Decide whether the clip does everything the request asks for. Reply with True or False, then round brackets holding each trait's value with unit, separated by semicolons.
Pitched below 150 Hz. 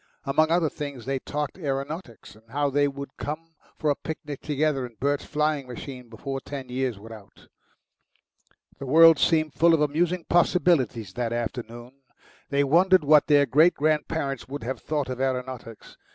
True (140 Hz)